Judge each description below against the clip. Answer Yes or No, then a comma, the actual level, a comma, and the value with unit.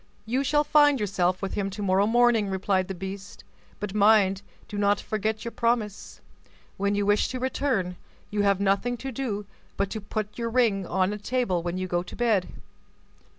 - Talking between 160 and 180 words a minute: No, average, 190 wpm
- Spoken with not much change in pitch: No, average, 3.2 semitones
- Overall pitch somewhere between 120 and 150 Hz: No, high, 205 Hz